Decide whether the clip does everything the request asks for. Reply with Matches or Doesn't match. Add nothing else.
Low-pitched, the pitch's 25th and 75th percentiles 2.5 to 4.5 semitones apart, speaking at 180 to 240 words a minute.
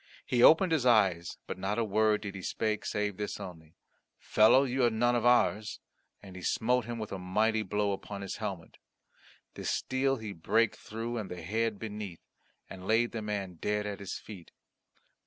Matches